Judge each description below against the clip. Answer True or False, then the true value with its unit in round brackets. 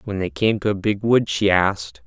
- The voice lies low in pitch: True (100 Hz)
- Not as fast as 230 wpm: False (260 wpm)